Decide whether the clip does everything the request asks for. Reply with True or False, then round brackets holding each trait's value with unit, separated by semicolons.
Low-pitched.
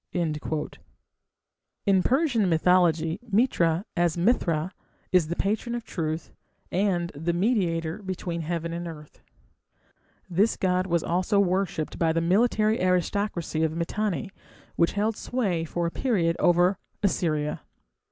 False (180 Hz)